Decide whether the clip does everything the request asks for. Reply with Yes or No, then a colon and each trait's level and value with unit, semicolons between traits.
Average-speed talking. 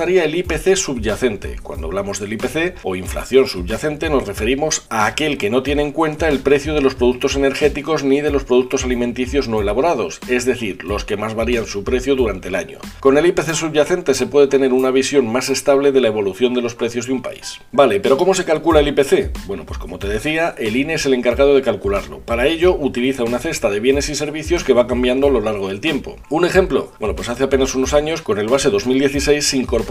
No: fast, 225 wpm